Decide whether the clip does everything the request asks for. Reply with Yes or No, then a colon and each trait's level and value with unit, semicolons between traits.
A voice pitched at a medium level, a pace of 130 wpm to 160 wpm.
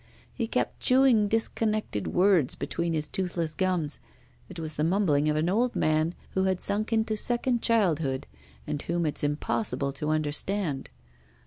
Yes: medium, 175 Hz; average, 150 wpm